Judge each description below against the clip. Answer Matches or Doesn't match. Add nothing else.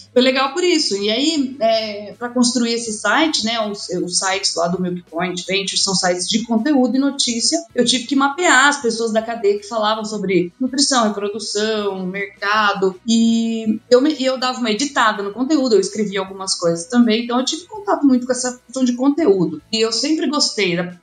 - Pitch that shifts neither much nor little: Matches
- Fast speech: Matches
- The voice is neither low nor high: Doesn't match